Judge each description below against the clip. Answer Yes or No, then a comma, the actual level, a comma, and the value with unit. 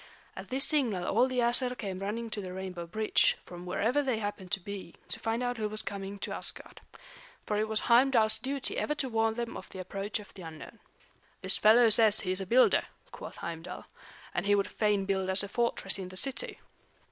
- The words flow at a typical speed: No, fast, 215 wpm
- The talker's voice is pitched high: Yes, high, 210 Hz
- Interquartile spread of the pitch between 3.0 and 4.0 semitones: Yes, average, 3.7 semitones